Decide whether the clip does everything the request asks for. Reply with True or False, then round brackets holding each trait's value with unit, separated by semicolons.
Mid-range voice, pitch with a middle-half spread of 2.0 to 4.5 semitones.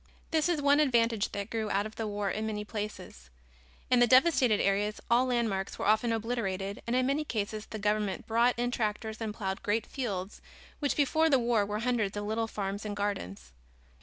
False (220 Hz; 2.9 semitones)